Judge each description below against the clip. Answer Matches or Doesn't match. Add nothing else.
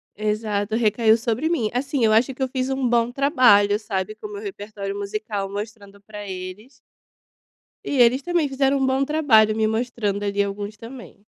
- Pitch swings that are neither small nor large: Matches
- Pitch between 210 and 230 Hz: Matches